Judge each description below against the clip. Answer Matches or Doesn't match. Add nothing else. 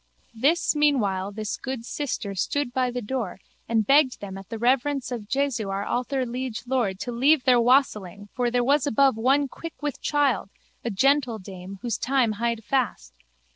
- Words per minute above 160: Matches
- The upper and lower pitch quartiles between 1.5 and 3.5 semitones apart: Doesn't match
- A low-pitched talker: Doesn't match